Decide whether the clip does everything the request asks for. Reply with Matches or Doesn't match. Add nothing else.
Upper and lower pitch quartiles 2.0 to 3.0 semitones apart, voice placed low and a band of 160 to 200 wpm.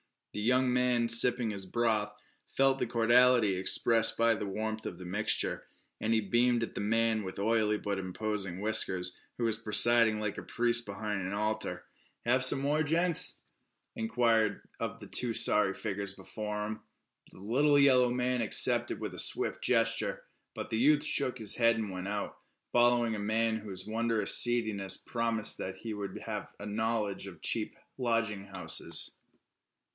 Matches